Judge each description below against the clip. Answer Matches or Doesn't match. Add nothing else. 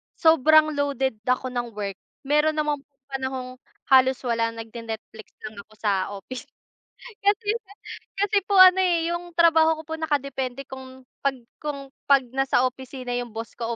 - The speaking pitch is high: Matches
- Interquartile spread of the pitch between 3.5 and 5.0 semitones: Matches